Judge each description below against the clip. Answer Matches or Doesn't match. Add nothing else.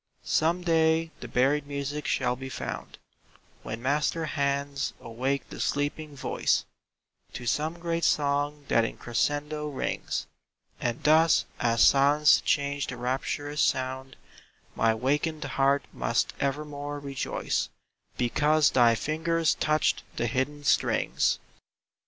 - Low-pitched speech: Doesn't match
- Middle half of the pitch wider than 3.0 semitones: Doesn't match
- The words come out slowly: Matches